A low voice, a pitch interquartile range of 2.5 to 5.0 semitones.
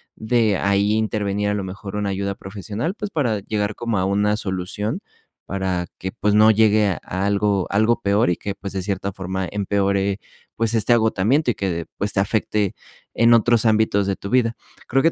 No: low, 105 Hz; narrow, 2.0 semitones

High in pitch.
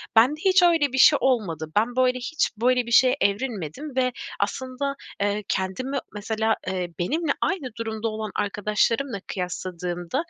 Yes: high, 230 Hz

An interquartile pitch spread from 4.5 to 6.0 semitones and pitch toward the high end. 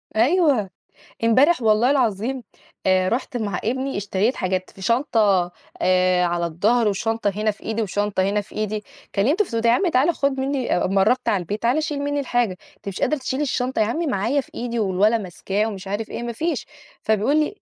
Yes: average, 4.9 semitones; high, 225 Hz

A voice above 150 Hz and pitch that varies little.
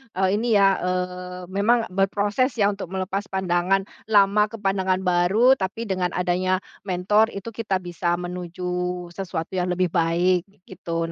Yes: medium, 185 Hz; narrow, 1.9 semitones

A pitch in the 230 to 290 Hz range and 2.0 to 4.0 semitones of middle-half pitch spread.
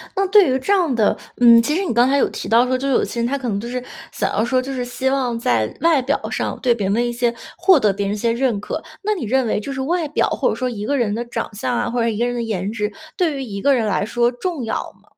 Yes: high, 245 Hz; average, 3.3 semitones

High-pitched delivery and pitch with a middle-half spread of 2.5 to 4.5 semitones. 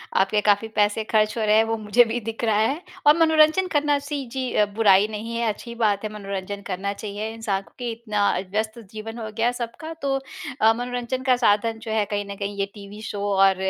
Yes: high, 220 Hz; average, 2.8 semitones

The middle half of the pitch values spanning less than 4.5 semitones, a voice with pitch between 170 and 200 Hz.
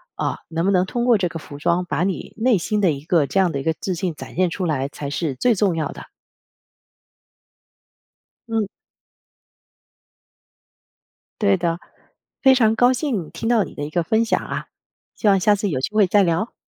No: average, 4.8 semitones; medium, 185 Hz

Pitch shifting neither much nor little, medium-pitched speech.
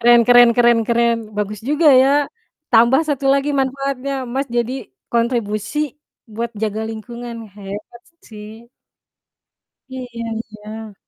No: average, 3.1 semitones; high, 235 Hz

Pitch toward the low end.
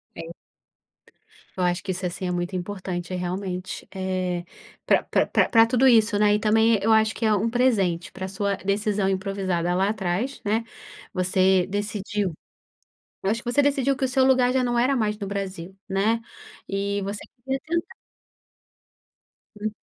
No: high, 200 Hz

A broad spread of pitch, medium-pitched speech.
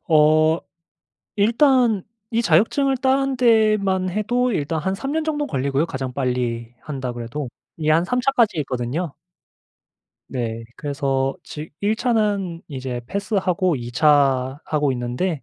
Yes: wide, 8.3 semitones; medium, 160 Hz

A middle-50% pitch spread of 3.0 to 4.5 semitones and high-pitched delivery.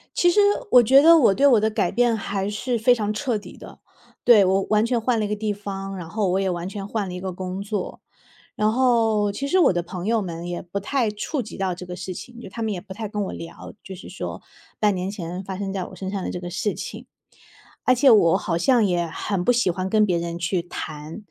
Yes: average, 3.6 semitones; high, 200 Hz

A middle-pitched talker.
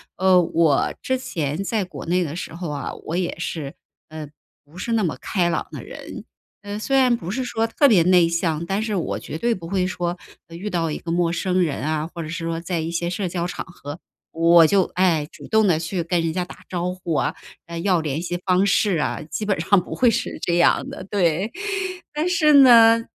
Yes: medium, 175 Hz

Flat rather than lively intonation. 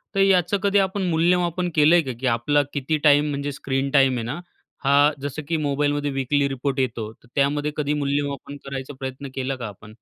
Yes: narrow, 2.1 semitones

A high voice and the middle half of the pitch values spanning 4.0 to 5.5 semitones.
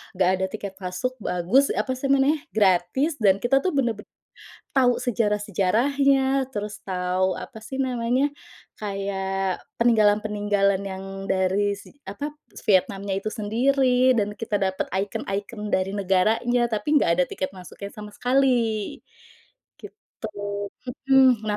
Yes: high, 210 Hz; average, 4.3 semitones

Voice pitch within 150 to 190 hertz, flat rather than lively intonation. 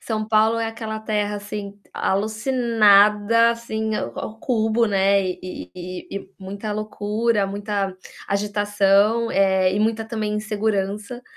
No: high, 210 Hz; narrow, 1.7 semitones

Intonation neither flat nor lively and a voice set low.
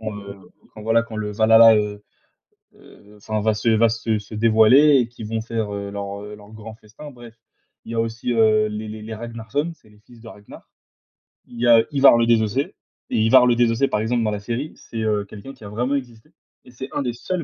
No: narrow, 1.9 semitones; low, 110 Hz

